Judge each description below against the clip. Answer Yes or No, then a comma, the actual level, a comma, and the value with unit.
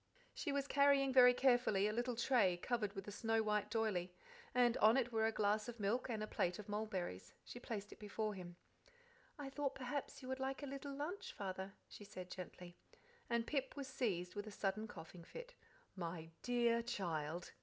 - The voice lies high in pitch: Yes, high, 220 Hz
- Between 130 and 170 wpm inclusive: No, average, 195 wpm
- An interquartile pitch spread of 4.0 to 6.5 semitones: Yes, average, 4.7 semitones